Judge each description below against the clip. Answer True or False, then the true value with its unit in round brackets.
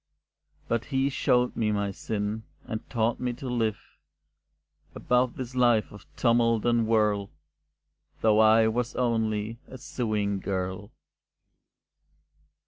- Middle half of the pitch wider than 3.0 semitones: False (2.4 semitones)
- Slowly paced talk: True (120 wpm)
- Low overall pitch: True (110 Hz)